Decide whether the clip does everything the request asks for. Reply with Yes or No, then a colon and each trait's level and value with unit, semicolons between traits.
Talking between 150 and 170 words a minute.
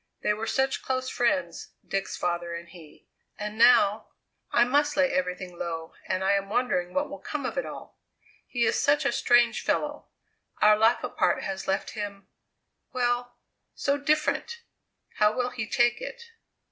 Yes: average, 165 wpm